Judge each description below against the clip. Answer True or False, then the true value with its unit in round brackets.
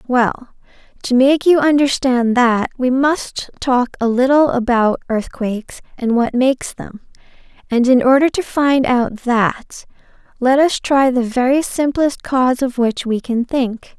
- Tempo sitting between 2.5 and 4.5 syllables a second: True (4.0 syllables/s)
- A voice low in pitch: False (255 Hz)